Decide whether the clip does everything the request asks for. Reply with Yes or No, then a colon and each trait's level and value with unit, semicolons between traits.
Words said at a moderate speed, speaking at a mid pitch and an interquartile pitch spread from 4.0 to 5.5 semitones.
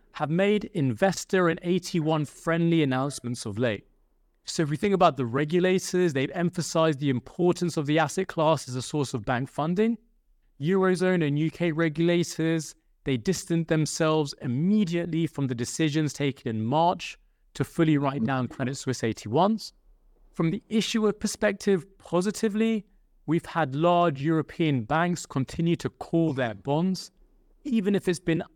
Yes: average, 145 wpm; medium, 165 Hz; average, 4.3 semitones